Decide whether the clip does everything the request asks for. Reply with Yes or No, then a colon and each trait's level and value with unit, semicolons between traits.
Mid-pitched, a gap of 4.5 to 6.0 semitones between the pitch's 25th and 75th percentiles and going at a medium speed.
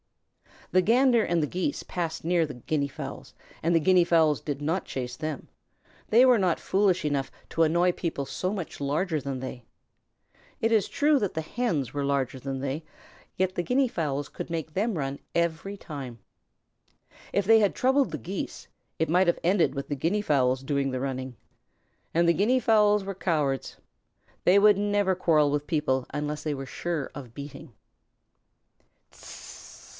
Yes: medium, 165 Hz; wide, 5.4 semitones; average, 170 wpm